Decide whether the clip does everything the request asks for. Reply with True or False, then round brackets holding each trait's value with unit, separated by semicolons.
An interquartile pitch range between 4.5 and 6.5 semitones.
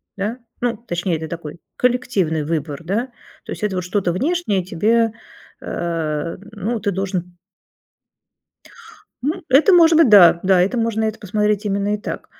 True (5.0 semitones)